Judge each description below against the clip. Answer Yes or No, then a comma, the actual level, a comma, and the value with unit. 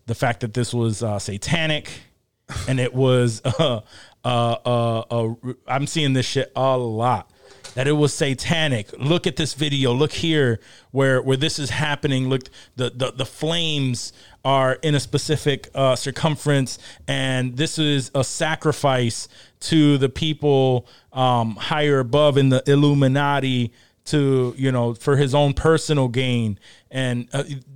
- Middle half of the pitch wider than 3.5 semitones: No, average, 2.9 semitones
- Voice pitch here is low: Yes, low, 130 Hz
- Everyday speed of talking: Yes, average, 150 wpm